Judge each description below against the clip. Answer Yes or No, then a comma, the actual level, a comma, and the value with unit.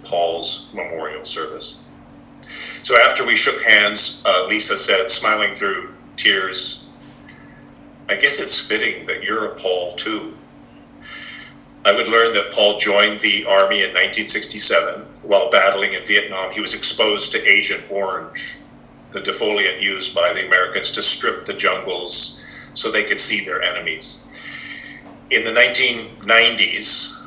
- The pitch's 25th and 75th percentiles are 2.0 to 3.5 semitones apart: Yes, average, 2.8 semitones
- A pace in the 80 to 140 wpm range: Yes, slow, 135 wpm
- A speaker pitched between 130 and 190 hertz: No, low, 100 Hz